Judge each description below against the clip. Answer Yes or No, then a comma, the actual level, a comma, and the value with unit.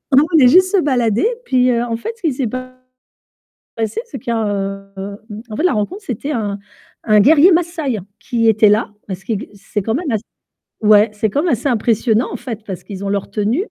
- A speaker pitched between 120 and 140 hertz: No, high, 235 Hz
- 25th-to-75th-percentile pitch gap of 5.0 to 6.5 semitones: Yes, average, 5.3 semitones